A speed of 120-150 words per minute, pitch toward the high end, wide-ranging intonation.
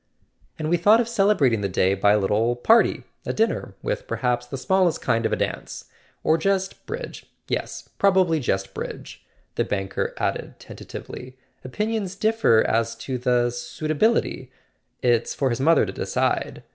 No: average, 145 wpm; low, 135 Hz; wide, 8.6 semitones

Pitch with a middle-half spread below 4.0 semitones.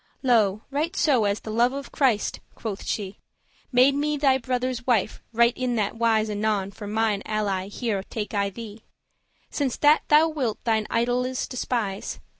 Yes: average, 3.4 semitones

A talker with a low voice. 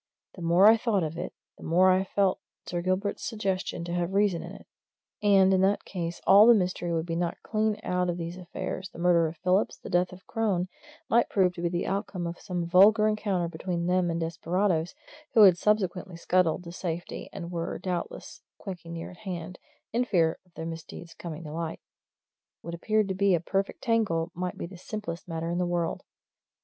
No: medium, 180 Hz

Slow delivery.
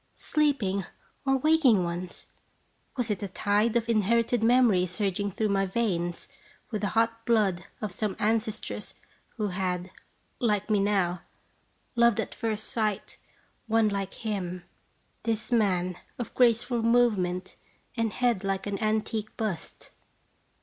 Yes: slow, 130 wpm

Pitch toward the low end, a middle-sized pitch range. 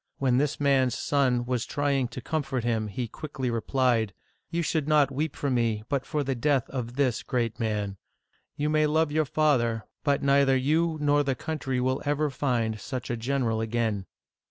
Yes: low, 130 Hz; average, 3.6 semitones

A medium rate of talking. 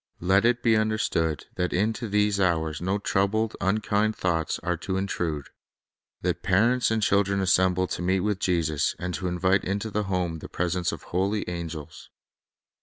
Yes: average, 170 wpm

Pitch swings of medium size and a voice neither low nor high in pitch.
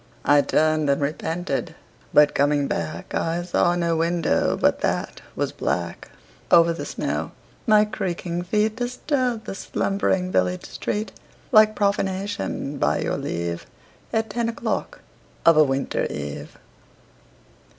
No: wide, 6.2 semitones; medium, 175 Hz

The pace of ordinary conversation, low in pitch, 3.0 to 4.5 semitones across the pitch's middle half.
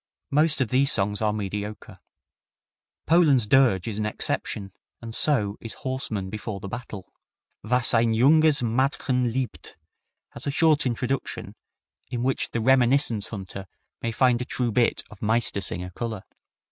Yes: average, 145 wpm; low, 115 Hz; average, 3.9 semitones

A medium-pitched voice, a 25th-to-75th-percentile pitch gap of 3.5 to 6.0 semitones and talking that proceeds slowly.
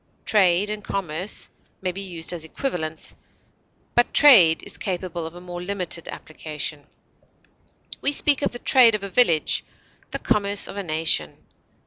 No: medium, 180 Hz; average, 4.2 semitones; average, 150 wpm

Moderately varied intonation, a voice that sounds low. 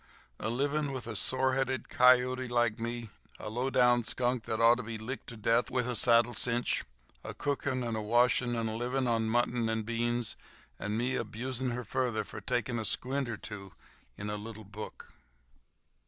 No: narrow, 2.1 semitones; low, 120 Hz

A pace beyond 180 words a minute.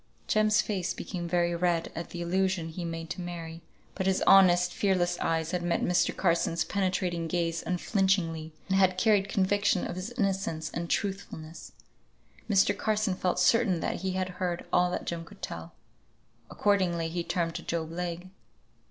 No: average, 165 wpm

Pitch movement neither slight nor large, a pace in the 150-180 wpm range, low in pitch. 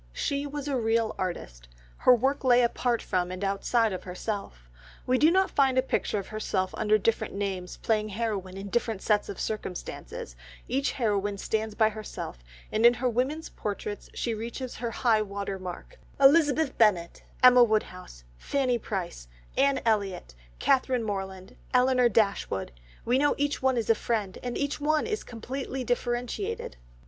No: average, 4.4 semitones; average, 160 wpm; high, 225 Hz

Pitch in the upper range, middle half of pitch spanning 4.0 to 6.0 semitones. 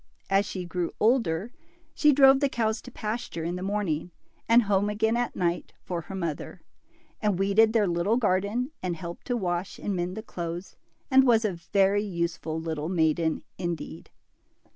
Yes: high, 195 Hz; average, 4.3 semitones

